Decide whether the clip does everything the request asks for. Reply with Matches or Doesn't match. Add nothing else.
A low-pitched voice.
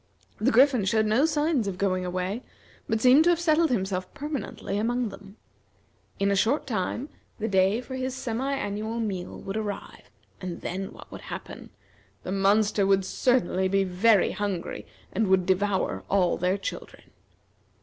Doesn't match